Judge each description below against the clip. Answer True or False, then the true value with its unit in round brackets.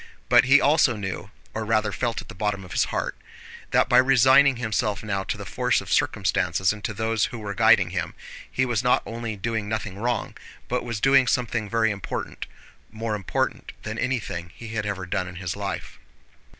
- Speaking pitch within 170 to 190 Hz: False (110 Hz)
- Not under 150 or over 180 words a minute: False (190 wpm)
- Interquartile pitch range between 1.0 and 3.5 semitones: True (3.0 semitones)